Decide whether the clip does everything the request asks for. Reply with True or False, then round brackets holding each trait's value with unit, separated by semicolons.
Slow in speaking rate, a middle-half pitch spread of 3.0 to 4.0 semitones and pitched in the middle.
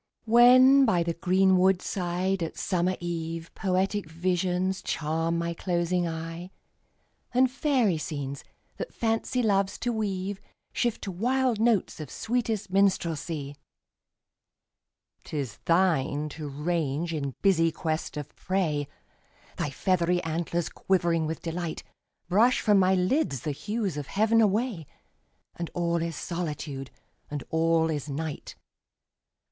True (125 wpm; 3.5 semitones; 175 Hz)